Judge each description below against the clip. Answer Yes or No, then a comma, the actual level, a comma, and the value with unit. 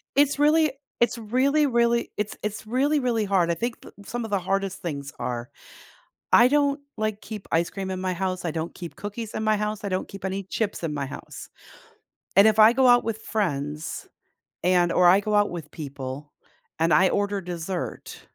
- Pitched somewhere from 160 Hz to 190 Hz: No, high, 200 Hz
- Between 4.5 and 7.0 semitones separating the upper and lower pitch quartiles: Yes, average, 4.8 semitones